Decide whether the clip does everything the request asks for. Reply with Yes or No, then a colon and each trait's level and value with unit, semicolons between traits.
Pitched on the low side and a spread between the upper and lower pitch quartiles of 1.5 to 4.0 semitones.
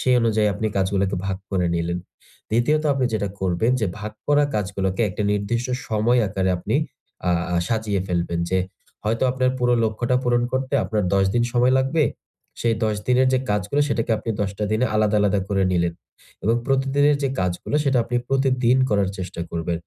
No: low, 110 Hz; average, 4.6 semitones